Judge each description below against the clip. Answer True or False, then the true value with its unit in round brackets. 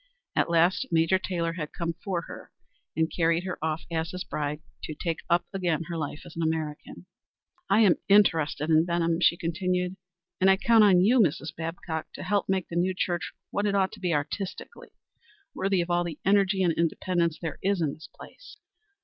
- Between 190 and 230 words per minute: True (195 wpm)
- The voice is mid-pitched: True (170 Hz)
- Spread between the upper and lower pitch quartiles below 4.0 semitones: True (2.6 semitones)